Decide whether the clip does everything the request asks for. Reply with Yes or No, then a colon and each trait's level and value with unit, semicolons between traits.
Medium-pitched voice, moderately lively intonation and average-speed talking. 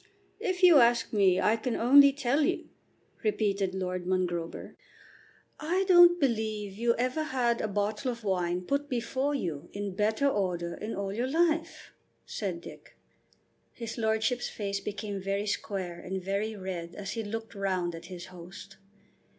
No: high, 210 Hz; average, 4.6 semitones; average, 155 wpm